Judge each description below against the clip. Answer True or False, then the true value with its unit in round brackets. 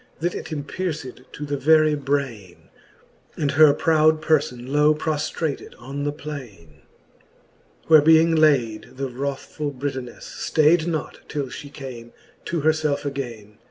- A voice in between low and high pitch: True (145 Hz)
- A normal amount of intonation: True (3.2 semitones)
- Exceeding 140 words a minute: False (135 wpm)